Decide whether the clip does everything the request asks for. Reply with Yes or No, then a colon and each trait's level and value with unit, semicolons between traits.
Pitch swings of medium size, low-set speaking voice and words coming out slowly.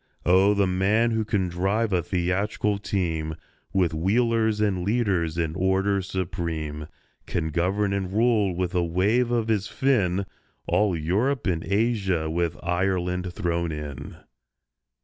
Yes: average, 3.4 semitones; very low, 95 Hz; slow, 130 wpm